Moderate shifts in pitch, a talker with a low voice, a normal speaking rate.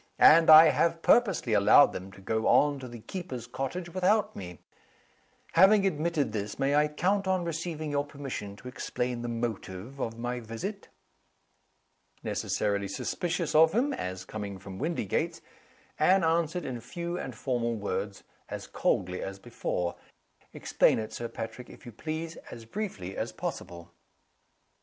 No: wide, 7.5 semitones; low, 130 Hz; average, 150 wpm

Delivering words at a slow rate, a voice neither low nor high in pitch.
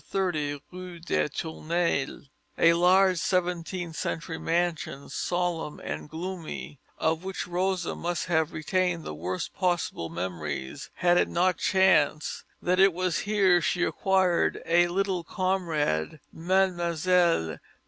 Yes: slow, 120 wpm; medium, 175 Hz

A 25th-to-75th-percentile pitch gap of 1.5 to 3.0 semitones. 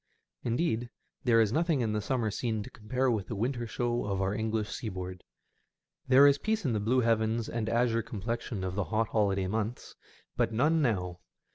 Yes: average, 2.7 semitones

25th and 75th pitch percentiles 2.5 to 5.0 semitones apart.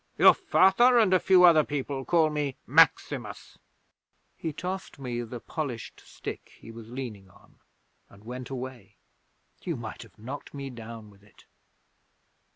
No: wide, 5.4 semitones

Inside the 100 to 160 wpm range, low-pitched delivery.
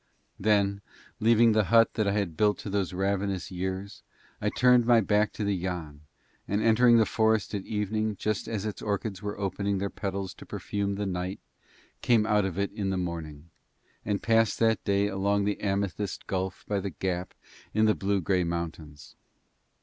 No: average, 180 wpm; low, 100 Hz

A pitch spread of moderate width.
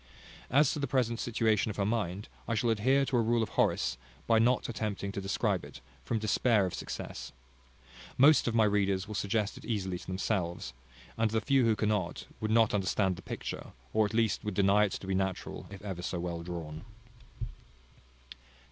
Yes: average, 3.0 semitones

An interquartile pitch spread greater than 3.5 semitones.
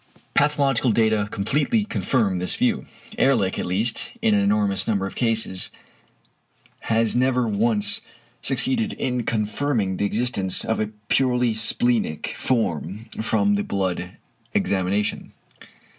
Yes: average, 4.0 semitones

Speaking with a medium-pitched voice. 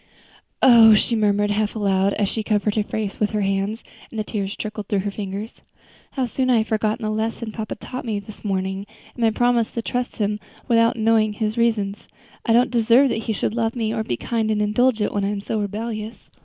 No: high, 215 Hz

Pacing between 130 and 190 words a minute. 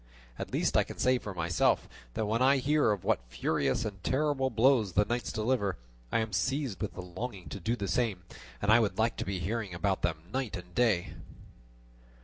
No: fast, 205 wpm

